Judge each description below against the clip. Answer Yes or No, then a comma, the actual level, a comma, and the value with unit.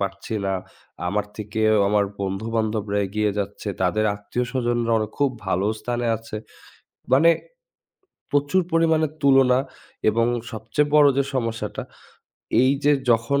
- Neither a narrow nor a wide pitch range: Yes, average, 4.4 semitones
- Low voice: Yes, low, 115 Hz